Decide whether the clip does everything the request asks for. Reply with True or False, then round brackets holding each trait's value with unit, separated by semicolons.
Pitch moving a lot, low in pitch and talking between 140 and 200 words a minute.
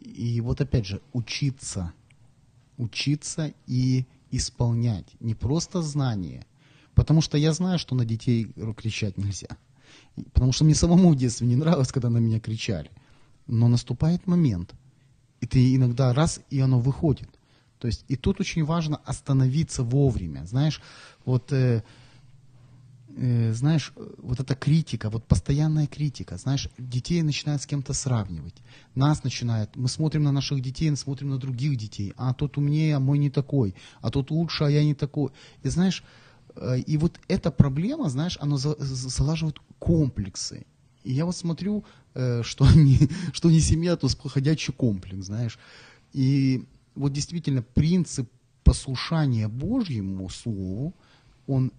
False (3.5 semitones; 130 Hz; 145 wpm)